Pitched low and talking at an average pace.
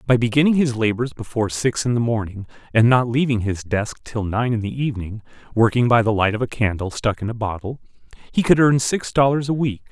No: low, 120 Hz; fast, 225 wpm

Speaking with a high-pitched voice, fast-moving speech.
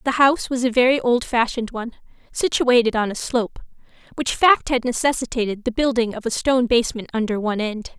No: high, 240 Hz; average, 180 wpm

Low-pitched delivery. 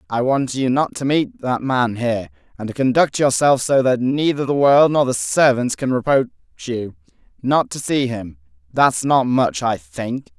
Yes: low, 120 Hz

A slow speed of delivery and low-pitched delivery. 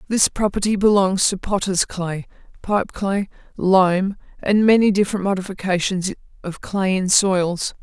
No: slow, 130 wpm; high, 190 Hz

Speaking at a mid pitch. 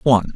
No: low, 115 Hz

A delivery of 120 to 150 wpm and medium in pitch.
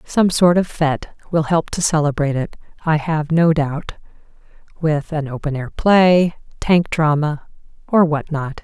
No: average, 160 wpm; medium, 155 Hz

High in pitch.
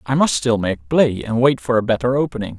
No: low, 120 Hz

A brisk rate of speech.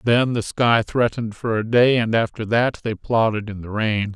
Yes: fast, 215 wpm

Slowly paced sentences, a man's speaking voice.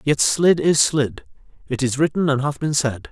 No: average, 195 wpm; male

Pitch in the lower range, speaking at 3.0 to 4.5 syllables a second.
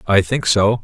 Yes: low, 105 Hz; 4.4 syllables/s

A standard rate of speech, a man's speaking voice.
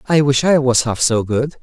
No: fast, 260 wpm; male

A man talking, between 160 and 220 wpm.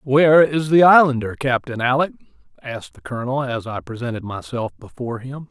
Yes: male; average, 165 wpm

